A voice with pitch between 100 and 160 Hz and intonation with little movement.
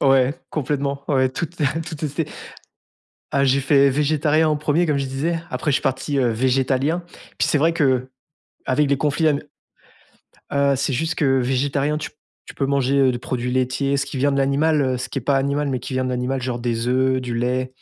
Yes: medium, 140 Hz; narrow, 2.2 semitones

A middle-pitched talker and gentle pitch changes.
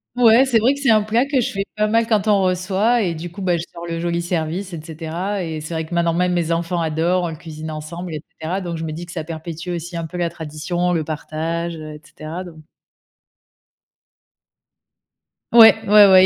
No: medium, 170 Hz; average, 3.1 semitones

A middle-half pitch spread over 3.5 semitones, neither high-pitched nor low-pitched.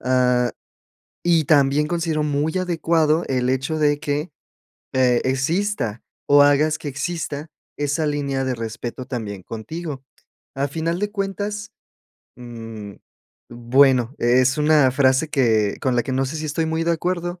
Yes: average, 4.0 semitones; medium, 145 Hz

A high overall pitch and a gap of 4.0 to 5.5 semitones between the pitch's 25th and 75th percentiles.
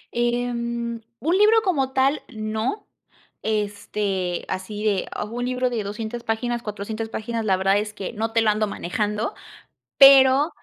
No: high, 225 Hz; average, 2.7 semitones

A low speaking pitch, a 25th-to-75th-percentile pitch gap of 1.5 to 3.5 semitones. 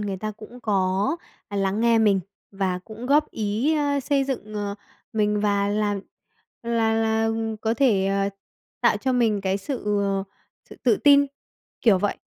No: high, 215 Hz; average, 2.9 semitones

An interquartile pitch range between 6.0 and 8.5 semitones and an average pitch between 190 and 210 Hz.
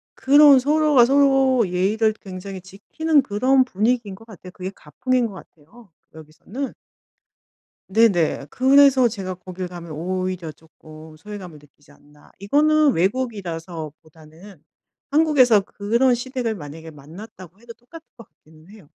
Yes: wide, 7.1 semitones; high, 200 Hz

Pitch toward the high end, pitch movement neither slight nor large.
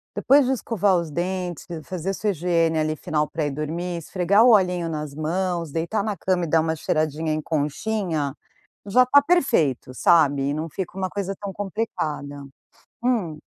No: medium, 170 Hz; average, 4.1 semitones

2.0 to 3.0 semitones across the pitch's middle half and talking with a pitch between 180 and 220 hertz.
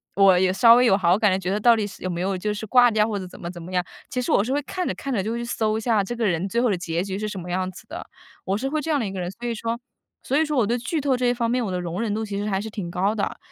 No: average, 4.1 semitones; high, 210 Hz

